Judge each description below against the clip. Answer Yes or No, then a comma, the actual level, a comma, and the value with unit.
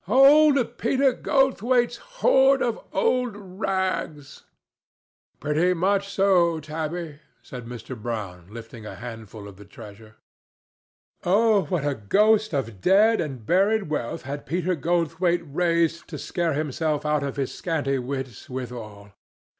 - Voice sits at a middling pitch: Yes, medium, 165 Hz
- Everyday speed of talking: No, slow, 130 wpm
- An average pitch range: No, wide, 7.6 semitones